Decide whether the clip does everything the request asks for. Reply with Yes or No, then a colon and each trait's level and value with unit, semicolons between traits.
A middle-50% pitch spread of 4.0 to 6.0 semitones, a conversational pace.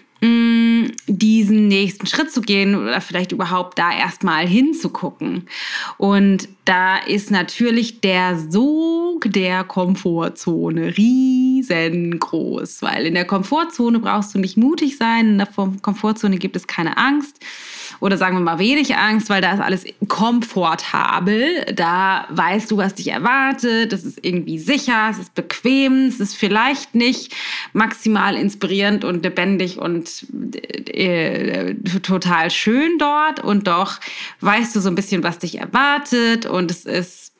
Yes: average, 4.3 semitones; average, 140 wpm